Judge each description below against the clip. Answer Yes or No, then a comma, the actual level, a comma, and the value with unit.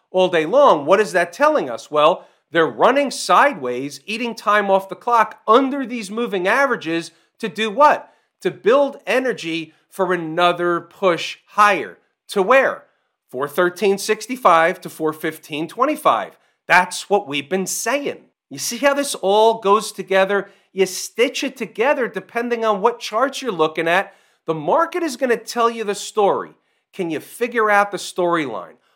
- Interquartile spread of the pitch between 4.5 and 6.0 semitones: Yes, average, 4.9 semitones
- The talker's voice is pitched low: No, high, 200 Hz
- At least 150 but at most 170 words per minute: Yes, average, 155 wpm